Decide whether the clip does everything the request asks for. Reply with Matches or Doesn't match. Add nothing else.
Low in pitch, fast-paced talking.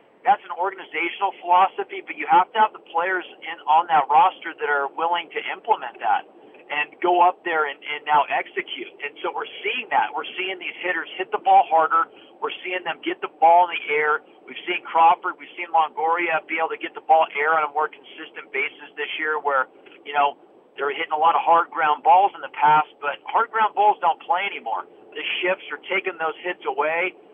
Doesn't match